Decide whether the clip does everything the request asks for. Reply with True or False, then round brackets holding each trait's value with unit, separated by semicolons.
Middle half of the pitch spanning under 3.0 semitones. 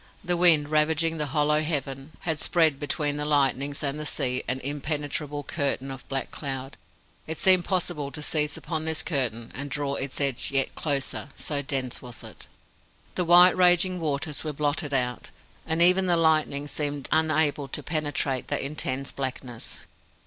True (2.6 semitones)